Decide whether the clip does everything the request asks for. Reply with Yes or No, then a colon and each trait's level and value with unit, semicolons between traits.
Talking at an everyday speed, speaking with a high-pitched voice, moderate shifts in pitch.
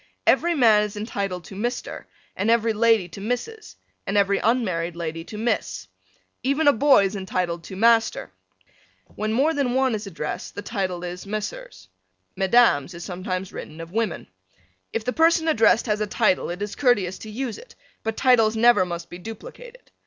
Yes: average, 175 wpm; high, 215 Hz; average, 4.6 semitones